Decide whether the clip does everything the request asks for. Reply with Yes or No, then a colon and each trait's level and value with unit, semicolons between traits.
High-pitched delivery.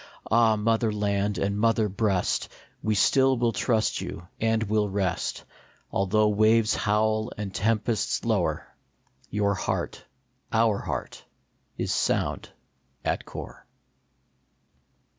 No: low, 110 Hz